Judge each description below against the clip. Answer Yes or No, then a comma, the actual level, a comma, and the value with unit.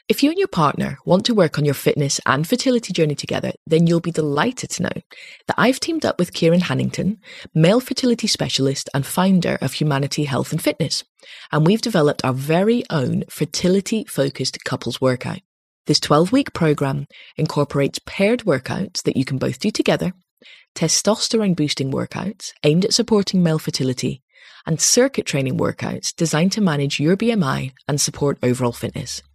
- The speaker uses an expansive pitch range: Yes, wide, 5.8 semitones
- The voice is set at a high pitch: No, medium, 160 Hz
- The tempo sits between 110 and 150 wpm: No, average, 170 wpm